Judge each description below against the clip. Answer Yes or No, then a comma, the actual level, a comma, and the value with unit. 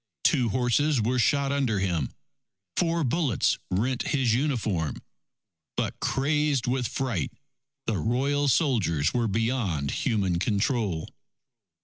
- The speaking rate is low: Yes, slow, 110 wpm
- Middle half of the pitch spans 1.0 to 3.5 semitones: No, wide, 5.6 semitones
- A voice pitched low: Yes, low, 120 Hz